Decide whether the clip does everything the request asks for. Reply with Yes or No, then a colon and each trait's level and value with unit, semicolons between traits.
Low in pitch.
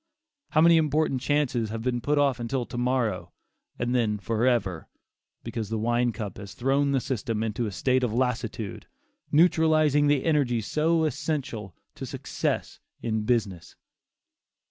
Yes: low, 125 Hz